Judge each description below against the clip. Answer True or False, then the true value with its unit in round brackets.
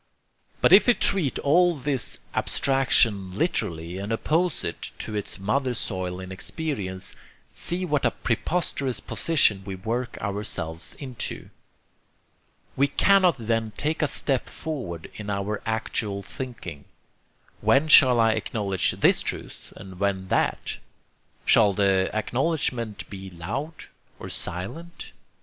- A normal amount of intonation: False (6.7 semitones)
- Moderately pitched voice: False (115 Hz)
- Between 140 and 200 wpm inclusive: False (125 wpm)